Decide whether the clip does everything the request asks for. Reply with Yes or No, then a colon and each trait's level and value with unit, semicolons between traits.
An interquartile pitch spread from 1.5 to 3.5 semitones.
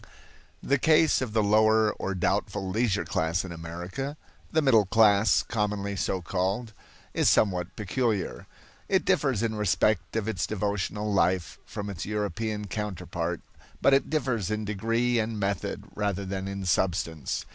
Yes: average, 2.7 semitones